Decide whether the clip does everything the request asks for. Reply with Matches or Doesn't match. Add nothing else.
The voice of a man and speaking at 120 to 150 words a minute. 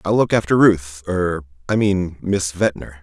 Matches